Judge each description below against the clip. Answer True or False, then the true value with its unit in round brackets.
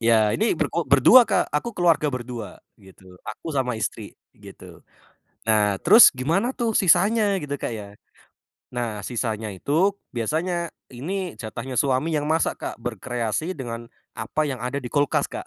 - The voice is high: False (135 Hz)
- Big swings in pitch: True (6.9 semitones)